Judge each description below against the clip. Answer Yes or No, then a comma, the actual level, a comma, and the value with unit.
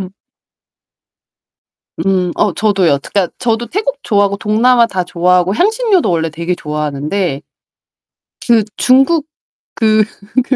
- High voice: Yes, high, 200 Hz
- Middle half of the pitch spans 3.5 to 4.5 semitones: No, wide, 5.5 semitones